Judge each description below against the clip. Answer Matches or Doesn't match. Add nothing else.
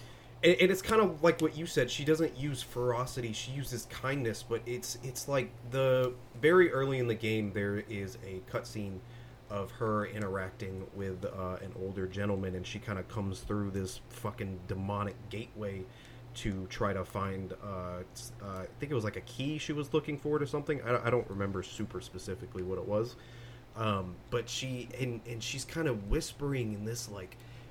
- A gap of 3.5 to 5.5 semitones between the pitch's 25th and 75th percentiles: Matches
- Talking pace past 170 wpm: Matches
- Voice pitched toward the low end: Matches